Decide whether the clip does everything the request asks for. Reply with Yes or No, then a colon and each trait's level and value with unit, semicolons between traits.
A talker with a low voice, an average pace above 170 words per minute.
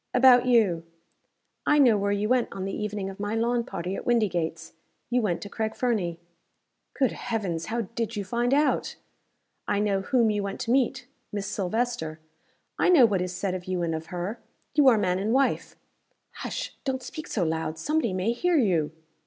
No: high, 210 Hz; average, 195 wpm